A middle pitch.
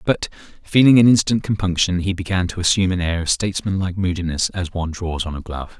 No: very low, 90 Hz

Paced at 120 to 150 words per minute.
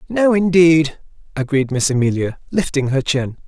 Yes: average, 140 wpm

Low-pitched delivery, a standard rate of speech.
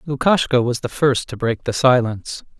Yes: low, 125 Hz; average, 185 wpm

